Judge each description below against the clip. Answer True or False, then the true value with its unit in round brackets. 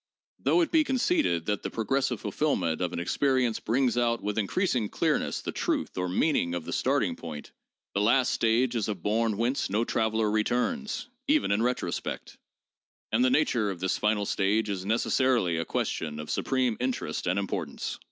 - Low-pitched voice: True (110 Hz)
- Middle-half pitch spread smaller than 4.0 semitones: False (4.7 semitones)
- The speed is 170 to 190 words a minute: True (180 wpm)